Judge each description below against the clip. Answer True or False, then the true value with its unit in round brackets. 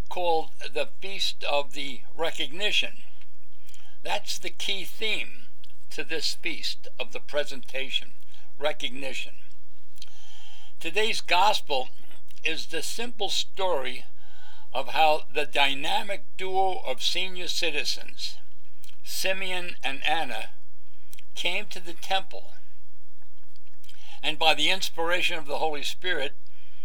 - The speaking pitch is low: False (155 Hz)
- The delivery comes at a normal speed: False (105 wpm)